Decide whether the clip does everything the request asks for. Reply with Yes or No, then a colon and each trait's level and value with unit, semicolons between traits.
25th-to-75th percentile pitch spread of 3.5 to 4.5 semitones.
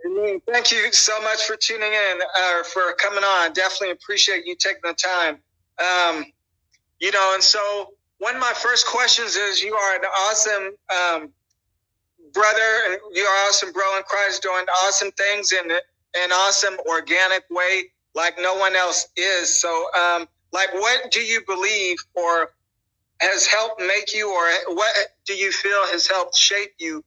No: narrow, 2.6 semitones